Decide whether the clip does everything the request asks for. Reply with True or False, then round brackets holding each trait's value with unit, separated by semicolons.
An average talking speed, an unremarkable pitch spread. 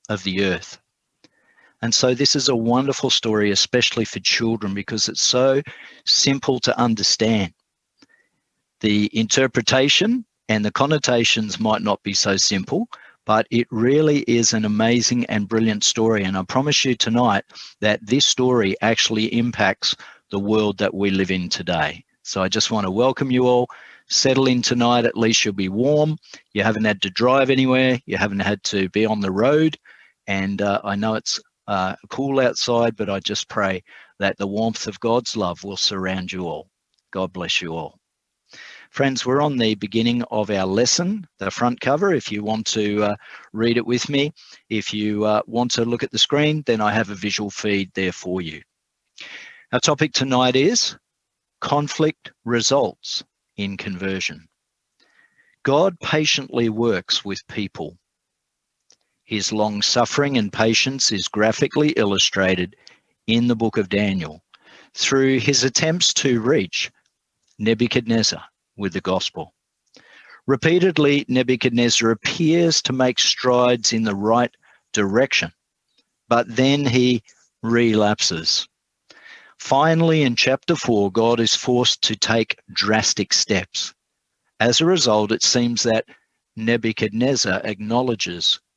True (145 wpm; 3.8 semitones)